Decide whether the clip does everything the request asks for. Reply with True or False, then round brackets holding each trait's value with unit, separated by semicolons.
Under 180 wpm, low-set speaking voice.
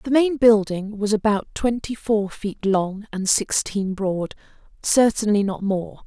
False (140 wpm; 210 Hz)